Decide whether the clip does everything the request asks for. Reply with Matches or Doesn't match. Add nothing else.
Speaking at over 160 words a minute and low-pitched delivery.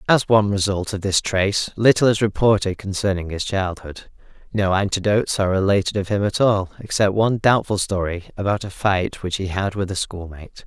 Matches